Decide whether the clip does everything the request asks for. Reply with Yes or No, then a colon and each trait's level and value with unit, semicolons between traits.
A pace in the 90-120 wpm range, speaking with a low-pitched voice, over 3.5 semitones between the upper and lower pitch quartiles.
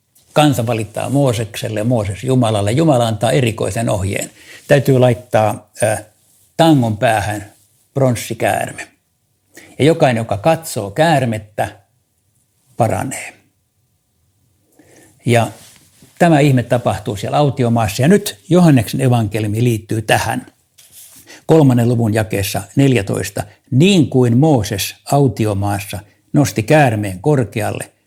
Yes: slow, 95 wpm; low, 120 Hz; average, 4.0 semitones